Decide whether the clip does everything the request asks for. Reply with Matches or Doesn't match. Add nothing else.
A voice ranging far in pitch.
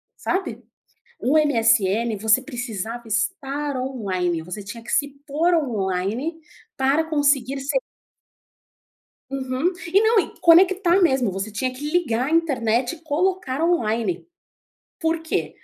Matches